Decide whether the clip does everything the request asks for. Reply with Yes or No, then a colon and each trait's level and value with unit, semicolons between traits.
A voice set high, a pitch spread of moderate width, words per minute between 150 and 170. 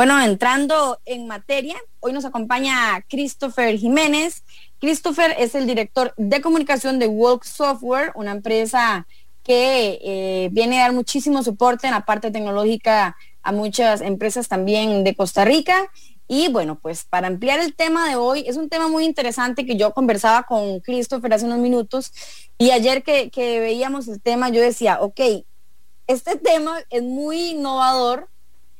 Yes: high, 245 Hz; average, 4.1 semitones; average, 155 wpm